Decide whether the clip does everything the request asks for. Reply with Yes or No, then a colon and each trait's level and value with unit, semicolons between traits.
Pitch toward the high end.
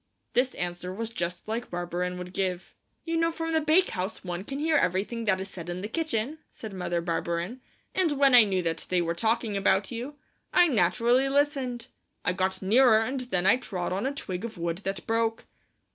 Yes: high, 215 Hz